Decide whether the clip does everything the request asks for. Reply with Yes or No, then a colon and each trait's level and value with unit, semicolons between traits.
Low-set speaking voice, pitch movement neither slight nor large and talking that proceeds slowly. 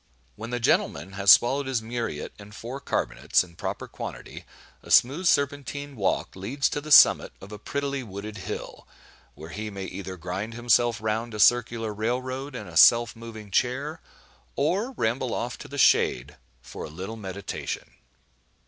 No: low, 115 Hz; average, 4.6 semitones; average, 165 wpm